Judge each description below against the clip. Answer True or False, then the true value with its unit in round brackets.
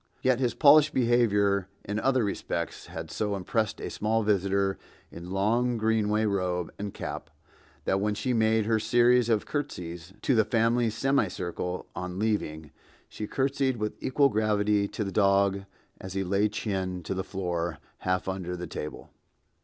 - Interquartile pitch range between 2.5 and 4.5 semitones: True (3.5 semitones)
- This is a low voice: True (105 Hz)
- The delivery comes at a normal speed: True (160 wpm)